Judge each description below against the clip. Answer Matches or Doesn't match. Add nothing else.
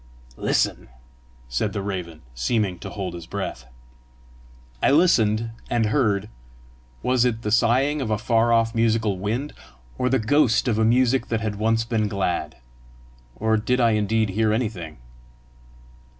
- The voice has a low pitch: Matches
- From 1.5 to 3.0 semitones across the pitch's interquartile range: Matches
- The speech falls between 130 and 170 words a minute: Matches